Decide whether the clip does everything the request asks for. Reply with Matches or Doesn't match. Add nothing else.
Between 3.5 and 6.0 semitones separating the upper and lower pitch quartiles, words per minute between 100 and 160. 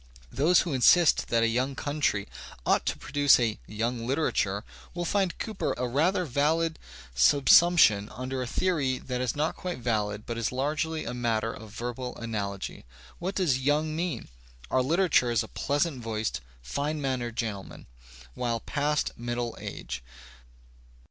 Matches